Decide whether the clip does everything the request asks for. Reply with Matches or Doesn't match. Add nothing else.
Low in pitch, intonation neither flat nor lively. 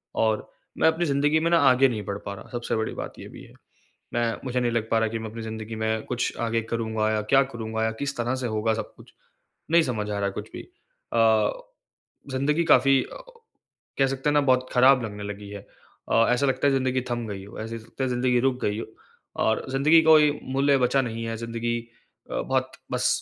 Matches